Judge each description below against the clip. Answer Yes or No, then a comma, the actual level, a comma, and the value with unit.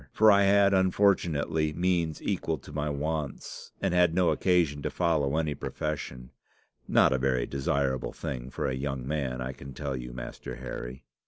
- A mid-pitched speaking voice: No, very low, 75 Hz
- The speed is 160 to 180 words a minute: Yes, average, 170 wpm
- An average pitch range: Yes, average, 4.7 semitones